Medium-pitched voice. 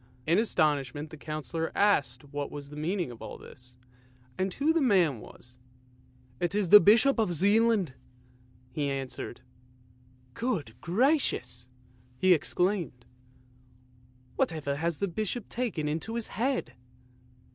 Yes: medium, 155 Hz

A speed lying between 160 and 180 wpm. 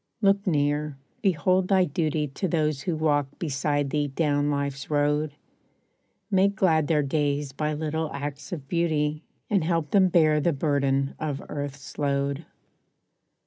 No: average, 145 wpm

